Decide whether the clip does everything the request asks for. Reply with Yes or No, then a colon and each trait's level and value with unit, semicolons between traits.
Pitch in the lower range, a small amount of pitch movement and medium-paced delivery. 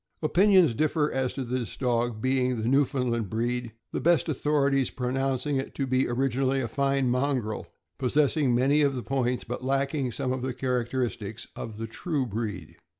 Yes: low, 130 Hz; narrow, 2.3 semitones; average, 170 wpm